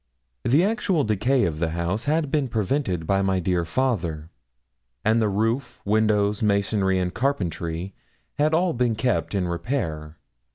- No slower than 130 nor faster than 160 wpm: Yes, average, 150 wpm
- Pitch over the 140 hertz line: No, low, 105 Hz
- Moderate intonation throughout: No, wide, 6.5 semitones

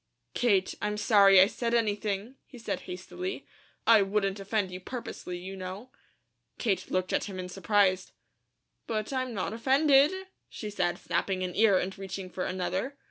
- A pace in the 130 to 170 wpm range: Yes, average, 160 wpm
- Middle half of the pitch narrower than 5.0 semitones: Yes, average, 3.5 semitones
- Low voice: No, high, 200 Hz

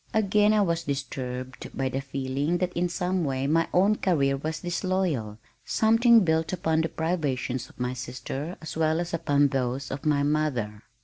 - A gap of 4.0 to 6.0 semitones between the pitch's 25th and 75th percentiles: Yes, average, 4.8 semitones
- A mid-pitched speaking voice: Yes, medium, 155 Hz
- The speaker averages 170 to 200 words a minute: Yes, average, 175 wpm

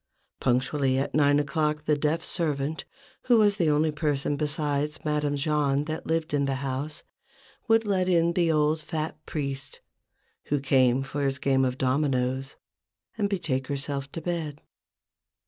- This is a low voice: No, medium, 145 Hz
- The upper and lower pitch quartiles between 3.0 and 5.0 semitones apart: No, narrow, 2.4 semitones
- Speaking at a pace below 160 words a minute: Yes, average, 150 wpm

